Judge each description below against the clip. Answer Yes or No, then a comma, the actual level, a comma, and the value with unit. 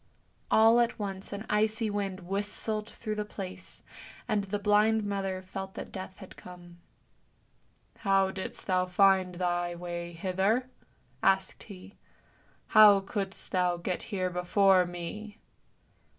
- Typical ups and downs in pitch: No, narrow, 2.3 semitones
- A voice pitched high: Yes, high, 195 Hz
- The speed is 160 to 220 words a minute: No, average, 140 wpm